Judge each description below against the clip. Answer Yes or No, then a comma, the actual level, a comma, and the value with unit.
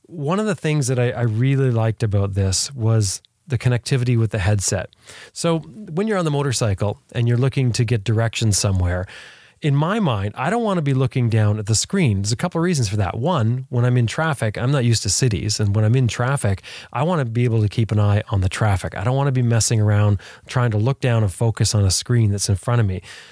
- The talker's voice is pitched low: Yes, low, 120 Hz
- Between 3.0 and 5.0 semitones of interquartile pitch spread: Yes, average, 4.3 semitones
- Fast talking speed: Yes, fast, 250 wpm